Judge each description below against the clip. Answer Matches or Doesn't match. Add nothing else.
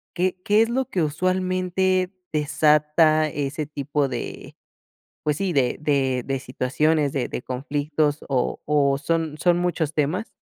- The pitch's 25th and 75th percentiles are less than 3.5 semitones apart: Doesn't match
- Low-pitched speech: Doesn't match